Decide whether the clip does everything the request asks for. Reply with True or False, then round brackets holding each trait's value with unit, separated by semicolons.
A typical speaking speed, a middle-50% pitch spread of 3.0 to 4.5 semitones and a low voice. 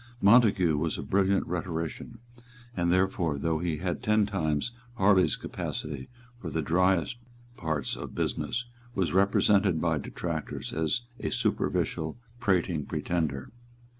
False (125 wpm; 3.6 semitones; 85 Hz)